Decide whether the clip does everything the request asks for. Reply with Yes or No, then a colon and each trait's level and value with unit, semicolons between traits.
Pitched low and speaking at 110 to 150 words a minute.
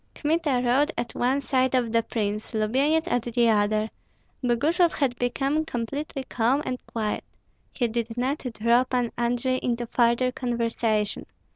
No: high, 245 Hz; average, 145 wpm